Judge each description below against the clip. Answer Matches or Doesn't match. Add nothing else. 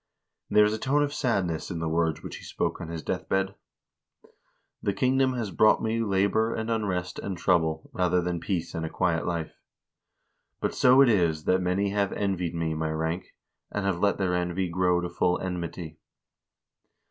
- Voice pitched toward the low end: Matches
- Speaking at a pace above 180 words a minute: Matches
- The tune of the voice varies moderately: Matches